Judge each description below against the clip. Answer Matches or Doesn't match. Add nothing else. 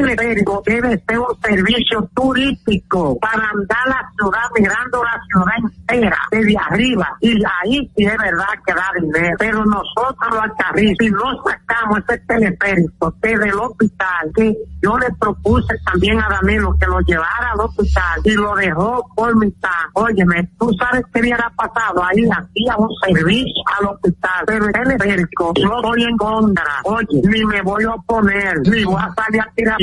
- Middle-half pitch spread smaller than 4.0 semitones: Matches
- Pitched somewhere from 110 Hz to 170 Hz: Doesn't match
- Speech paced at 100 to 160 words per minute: Doesn't match